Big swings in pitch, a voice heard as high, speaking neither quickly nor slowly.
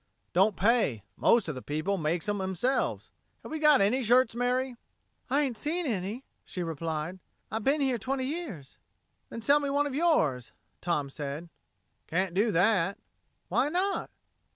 Yes: wide, 7.9 semitones; high, 220 Hz; average, 165 wpm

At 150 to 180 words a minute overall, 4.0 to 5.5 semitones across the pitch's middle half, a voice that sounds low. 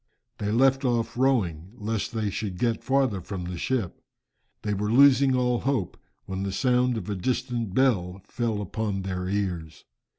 Yes: average, 165 wpm; average, 4.7 semitones; low, 110 Hz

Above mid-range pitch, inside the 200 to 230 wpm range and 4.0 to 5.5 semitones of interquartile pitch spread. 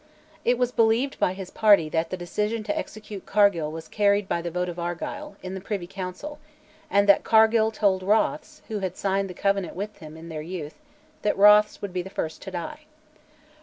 No: high, 195 Hz; fast, 205 wpm; average, 3.3 semitones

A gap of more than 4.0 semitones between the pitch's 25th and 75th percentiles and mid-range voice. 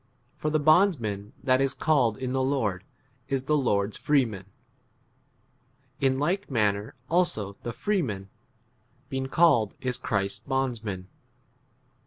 No: wide, 5.6 semitones; low, 130 Hz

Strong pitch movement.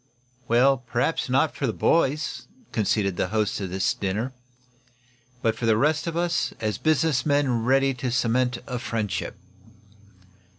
No: average, 3.9 semitones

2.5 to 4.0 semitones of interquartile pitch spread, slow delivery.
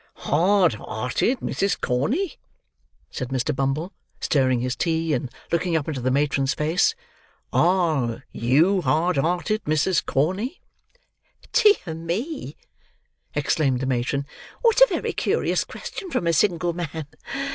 No: average, 5.3 semitones; slow, 125 wpm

